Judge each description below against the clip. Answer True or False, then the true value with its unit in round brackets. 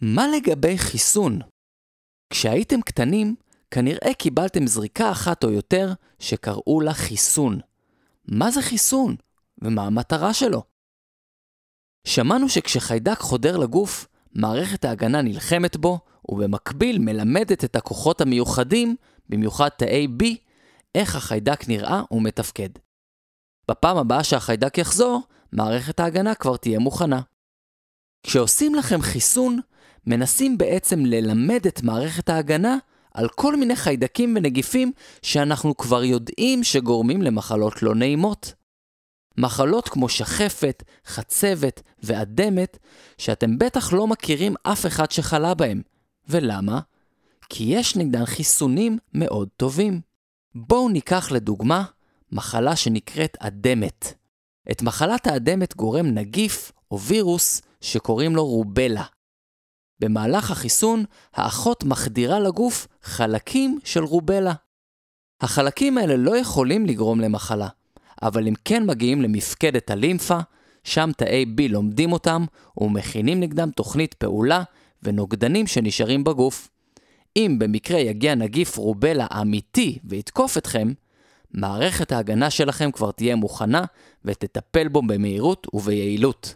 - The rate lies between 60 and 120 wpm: True (110 wpm)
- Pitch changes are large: True (8.8 semitones)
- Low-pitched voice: False (145 Hz)